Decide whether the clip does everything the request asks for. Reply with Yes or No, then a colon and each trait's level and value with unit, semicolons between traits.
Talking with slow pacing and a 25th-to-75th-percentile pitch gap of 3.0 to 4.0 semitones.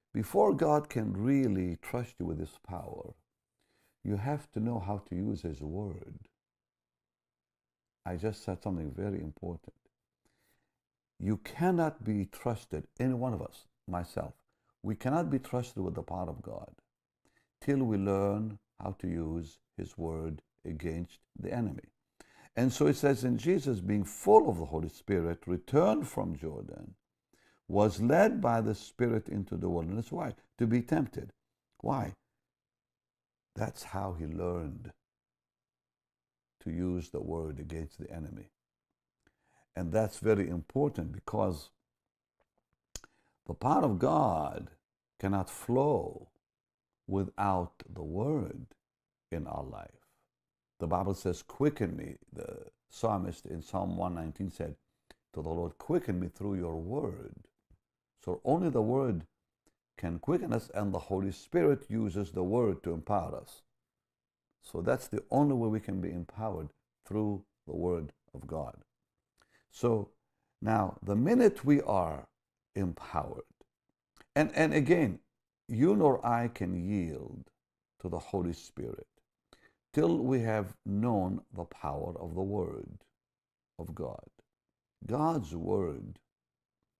No: slow, 130 wpm; wide, 5.5 semitones